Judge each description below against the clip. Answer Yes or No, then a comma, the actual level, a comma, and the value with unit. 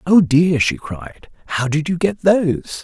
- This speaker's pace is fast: No, average, 190 wpm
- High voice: No, medium, 160 Hz